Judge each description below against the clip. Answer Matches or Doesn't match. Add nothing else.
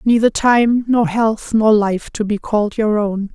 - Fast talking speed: Doesn't match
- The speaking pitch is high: Matches